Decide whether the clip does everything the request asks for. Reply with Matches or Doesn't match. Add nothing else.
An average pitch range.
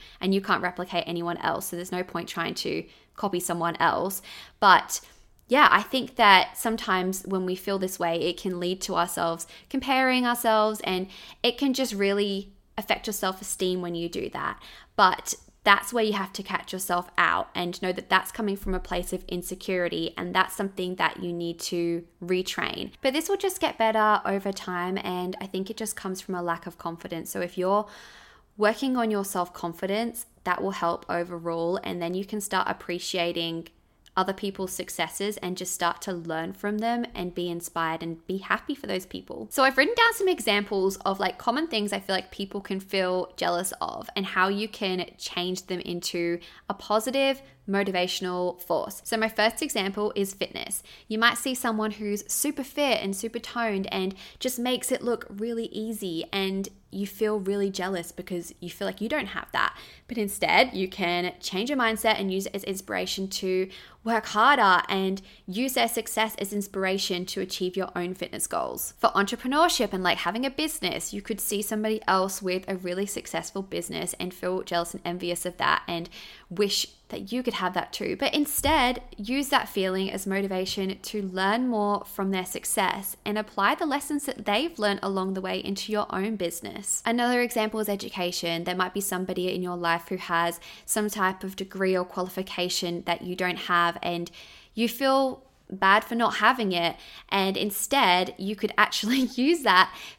Matches